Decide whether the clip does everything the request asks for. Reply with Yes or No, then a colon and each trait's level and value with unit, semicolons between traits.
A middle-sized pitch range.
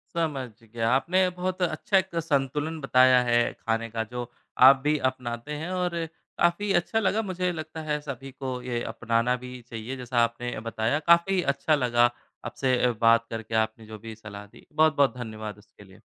No: wide, 5.8 semitones